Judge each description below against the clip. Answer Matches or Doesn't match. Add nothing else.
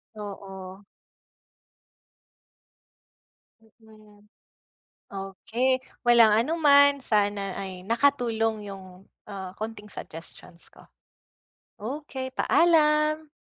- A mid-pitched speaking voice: Doesn't match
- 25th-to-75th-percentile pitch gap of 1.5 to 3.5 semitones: Doesn't match